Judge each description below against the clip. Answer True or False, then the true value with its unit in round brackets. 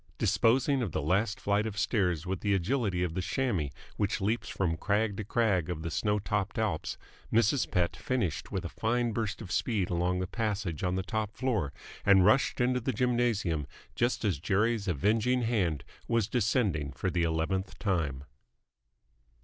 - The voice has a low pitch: True (100 Hz)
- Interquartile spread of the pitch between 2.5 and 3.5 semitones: False (4.2 semitones)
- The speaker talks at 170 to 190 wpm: True (175 wpm)